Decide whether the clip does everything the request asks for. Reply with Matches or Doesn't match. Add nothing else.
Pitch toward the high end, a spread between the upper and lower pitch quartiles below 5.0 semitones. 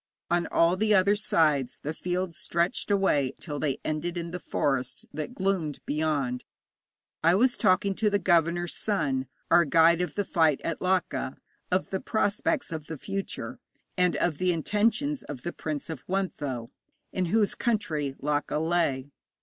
Doesn't match